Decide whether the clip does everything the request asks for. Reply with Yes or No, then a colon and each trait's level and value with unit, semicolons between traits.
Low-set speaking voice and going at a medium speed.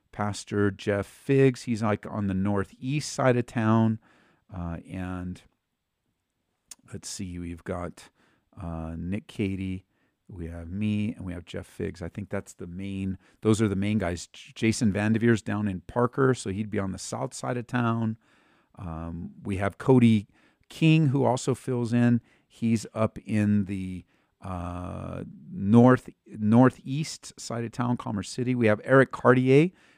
Yes: low, 105 Hz; average, 155 wpm